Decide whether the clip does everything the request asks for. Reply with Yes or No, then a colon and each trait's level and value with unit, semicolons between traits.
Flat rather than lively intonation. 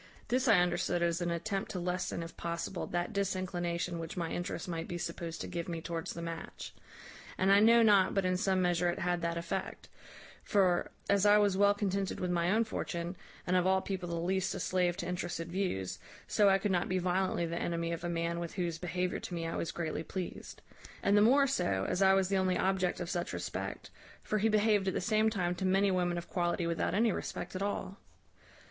Yes: narrow, 2.3 semitones